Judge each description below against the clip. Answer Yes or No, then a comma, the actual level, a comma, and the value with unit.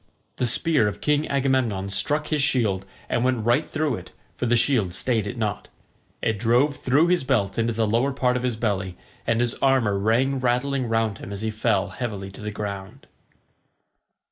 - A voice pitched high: No, low, 115 Hz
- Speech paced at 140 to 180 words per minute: No, average, 190 wpm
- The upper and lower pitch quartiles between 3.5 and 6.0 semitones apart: Yes, average, 4.1 semitones